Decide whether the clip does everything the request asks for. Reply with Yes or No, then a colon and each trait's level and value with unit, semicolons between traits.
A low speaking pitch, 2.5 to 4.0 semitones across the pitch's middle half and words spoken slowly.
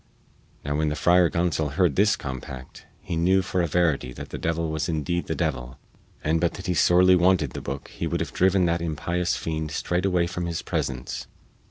No: very low, 85 Hz; average, 2.8 semitones; average, 200 wpm